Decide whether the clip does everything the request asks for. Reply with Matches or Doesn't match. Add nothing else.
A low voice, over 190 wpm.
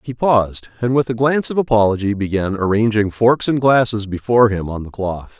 Matches